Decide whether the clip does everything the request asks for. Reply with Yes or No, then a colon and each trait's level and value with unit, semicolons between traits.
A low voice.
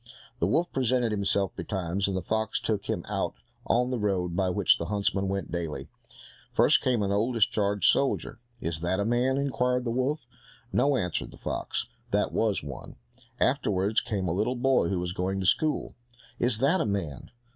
Yes: low, 100 Hz